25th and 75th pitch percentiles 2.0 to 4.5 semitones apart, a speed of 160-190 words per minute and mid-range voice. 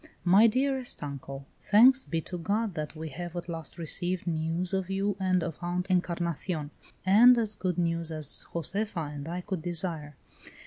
Yes: average, 3.1 semitones; average, 170 wpm; medium, 175 Hz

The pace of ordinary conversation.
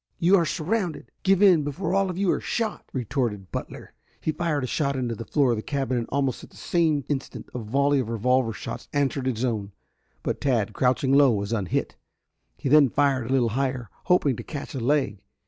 No: fast, 210 wpm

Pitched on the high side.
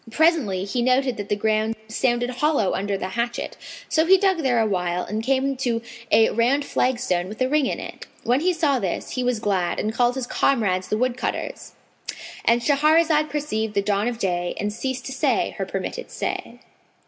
Yes: high, 240 Hz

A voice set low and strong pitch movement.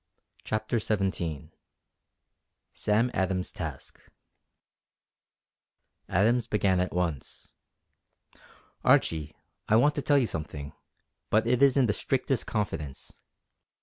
Yes: low, 105 Hz; wide, 6.2 semitones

